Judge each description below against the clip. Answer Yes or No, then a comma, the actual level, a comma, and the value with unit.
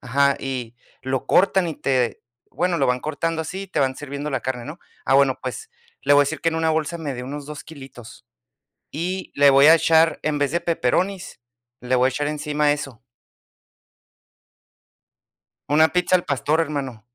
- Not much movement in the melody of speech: No, average, 3.4 semitones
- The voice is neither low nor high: Yes, medium, 145 Hz